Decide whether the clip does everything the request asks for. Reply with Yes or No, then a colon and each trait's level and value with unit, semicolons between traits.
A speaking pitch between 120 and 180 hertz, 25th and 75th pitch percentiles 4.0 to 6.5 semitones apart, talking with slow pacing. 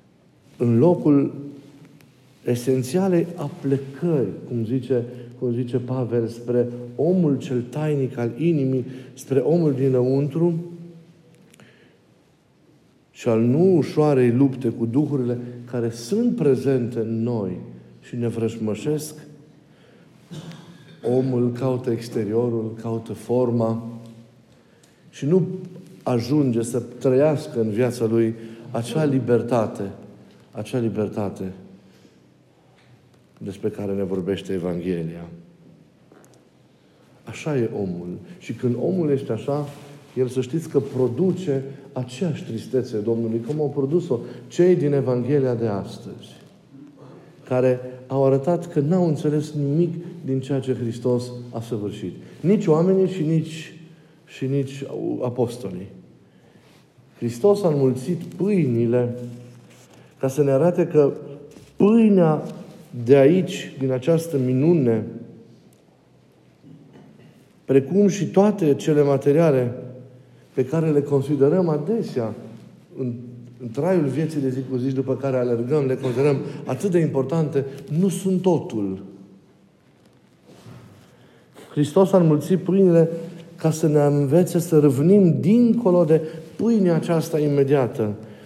Yes: low, 135 Hz; average, 4.9 semitones; slow, 105 wpm